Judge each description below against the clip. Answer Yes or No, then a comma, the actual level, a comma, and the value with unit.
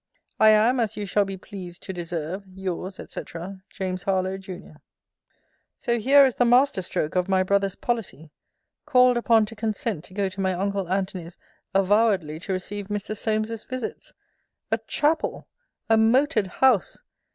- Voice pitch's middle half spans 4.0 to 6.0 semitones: No, average, 3.3 semitones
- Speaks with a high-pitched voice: Yes, high, 200 Hz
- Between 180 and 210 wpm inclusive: No, average, 155 wpm